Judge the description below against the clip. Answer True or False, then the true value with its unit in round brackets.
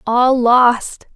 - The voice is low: False (245 Hz)